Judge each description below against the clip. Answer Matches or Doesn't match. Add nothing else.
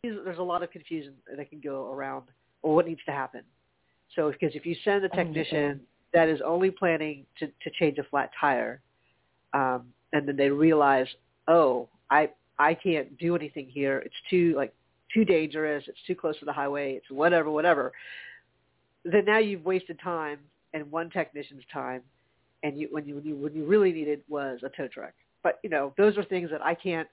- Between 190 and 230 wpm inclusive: Matches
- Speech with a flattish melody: Doesn't match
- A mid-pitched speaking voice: Matches